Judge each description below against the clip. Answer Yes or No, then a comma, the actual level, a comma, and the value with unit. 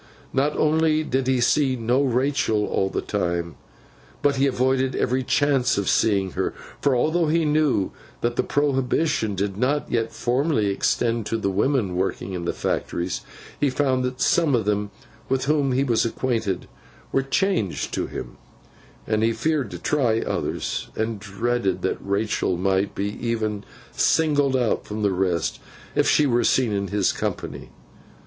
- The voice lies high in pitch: No, low, 120 Hz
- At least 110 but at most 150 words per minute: No, average, 165 wpm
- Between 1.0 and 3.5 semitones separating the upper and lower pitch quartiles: No, average, 5.3 semitones